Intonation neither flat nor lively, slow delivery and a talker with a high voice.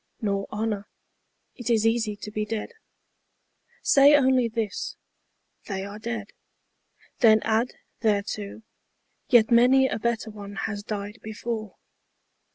No: narrow, 2.2 semitones; slow, 130 wpm; high, 220 Hz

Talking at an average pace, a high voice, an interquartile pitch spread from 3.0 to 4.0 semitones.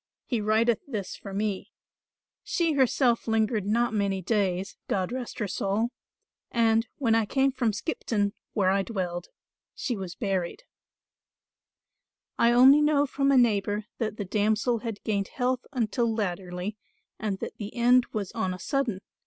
Yes: average, 155 wpm; high, 220 Hz; average, 3.4 semitones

